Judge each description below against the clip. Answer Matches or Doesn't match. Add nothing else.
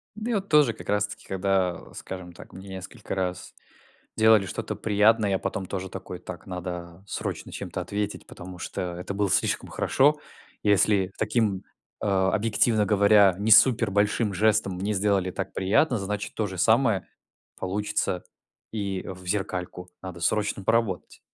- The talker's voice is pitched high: Doesn't match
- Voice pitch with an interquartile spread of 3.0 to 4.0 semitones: Doesn't match